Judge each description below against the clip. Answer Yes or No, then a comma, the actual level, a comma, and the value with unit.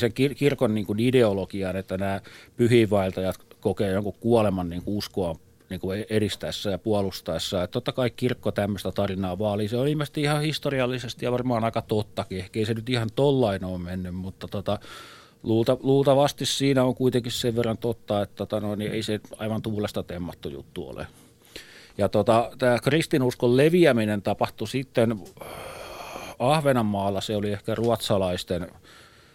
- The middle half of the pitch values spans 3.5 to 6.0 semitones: Yes, average, 3.9 semitones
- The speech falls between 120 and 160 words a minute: Yes, average, 145 wpm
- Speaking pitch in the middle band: No, low, 110 Hz